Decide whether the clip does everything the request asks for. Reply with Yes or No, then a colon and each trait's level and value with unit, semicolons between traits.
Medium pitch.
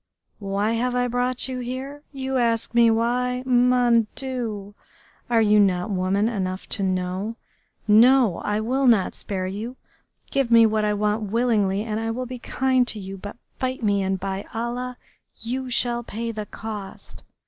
No: high, 230 Hz